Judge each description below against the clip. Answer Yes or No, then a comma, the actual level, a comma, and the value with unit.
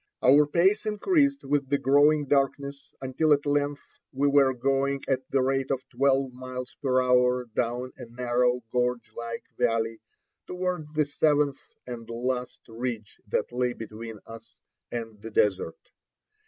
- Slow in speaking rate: No, average, 145 wpm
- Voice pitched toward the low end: Yes, low, 130 Hz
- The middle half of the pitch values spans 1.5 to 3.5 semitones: Yes, average, 2.9 semitones